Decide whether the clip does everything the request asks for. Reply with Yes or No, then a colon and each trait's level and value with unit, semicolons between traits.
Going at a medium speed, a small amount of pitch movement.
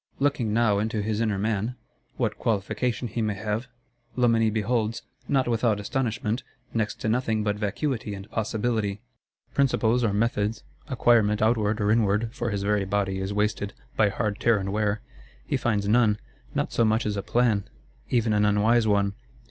Yes: average, 165 wpm; narrow, 2.1 semitones